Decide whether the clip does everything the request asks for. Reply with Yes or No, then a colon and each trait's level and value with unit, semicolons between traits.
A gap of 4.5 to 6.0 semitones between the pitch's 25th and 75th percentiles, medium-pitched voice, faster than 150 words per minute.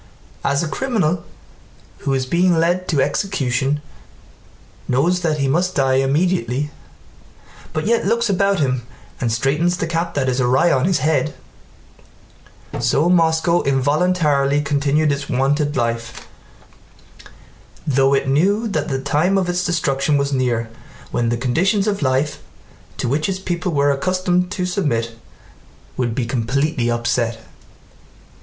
No: average, 5.0 semitones; medium, 145 Hz; slow, 135 wpm